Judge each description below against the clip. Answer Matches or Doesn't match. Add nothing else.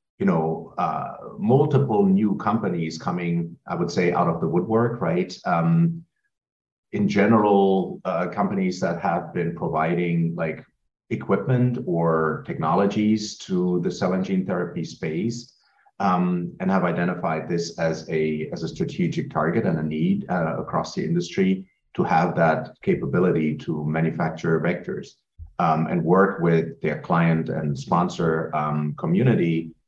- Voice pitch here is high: Doesn't match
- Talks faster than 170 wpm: Doesn't match